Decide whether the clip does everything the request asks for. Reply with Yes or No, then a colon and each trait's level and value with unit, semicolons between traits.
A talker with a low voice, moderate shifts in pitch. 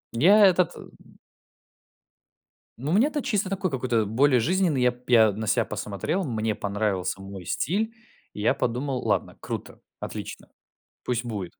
No: low, 125 Hz; wide, 9.0 semitones